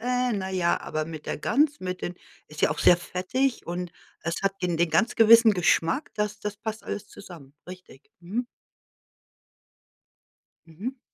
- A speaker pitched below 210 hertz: Yes, high, 190 Hz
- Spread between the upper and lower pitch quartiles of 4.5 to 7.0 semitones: Yes, average, 4.8 semitones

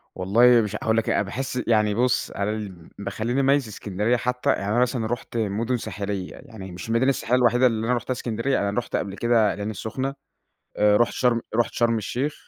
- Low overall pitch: Yes, low, 115 Hz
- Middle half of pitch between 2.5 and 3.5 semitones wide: Yes, average, 3.0 semitones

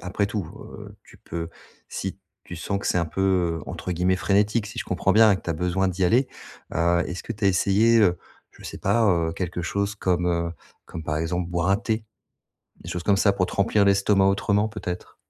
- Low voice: Yes, very low, 95 Hz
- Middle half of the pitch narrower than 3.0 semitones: Yes, narrow, 2.6 semitones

